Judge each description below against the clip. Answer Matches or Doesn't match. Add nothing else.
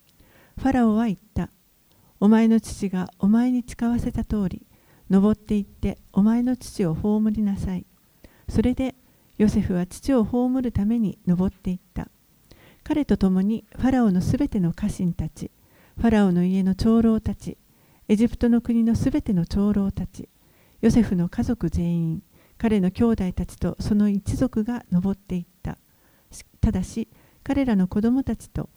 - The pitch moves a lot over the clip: Doesn't match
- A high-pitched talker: Matches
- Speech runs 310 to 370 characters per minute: Doesn't match